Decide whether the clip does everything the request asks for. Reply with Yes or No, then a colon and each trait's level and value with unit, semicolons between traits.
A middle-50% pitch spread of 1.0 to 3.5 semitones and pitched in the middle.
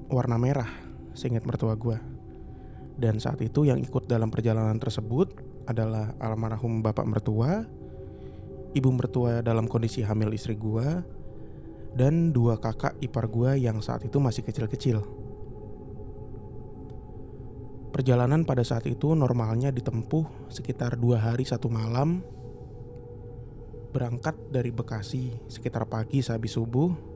No: average, 2.8 semitones; low, 120 Hz